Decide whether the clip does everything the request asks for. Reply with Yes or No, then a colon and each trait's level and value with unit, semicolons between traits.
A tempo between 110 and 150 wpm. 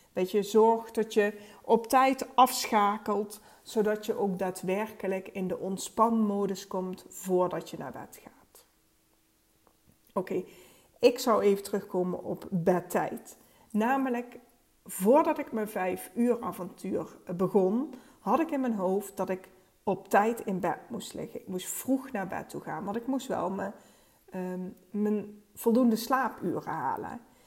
Yes: average, 145 wpm